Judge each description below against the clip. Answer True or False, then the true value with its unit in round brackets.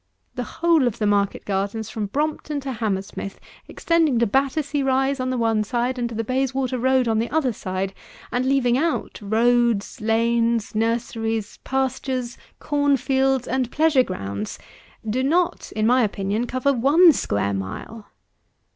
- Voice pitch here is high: True (245 Hz)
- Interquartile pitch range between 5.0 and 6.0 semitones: False (3.5 semitones)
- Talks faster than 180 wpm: False (155 wpm)